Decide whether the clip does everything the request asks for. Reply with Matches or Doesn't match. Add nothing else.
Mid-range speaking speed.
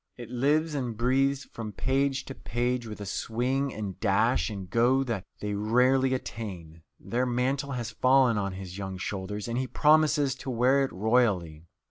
Matches